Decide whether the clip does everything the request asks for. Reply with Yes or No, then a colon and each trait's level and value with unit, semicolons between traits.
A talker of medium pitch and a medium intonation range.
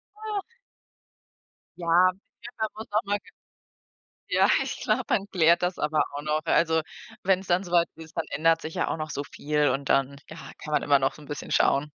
Yes: medium, 160 Hz; average, 3.6 semitones